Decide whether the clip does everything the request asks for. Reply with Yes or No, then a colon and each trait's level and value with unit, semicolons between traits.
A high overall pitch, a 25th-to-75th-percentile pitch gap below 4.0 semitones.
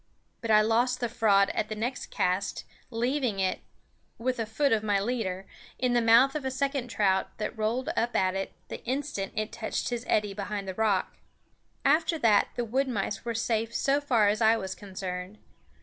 Yes: high, 225 Hz; average, 3.5 semitones